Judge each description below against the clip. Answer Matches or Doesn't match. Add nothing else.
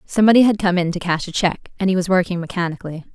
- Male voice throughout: Doesn't match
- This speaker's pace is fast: Matches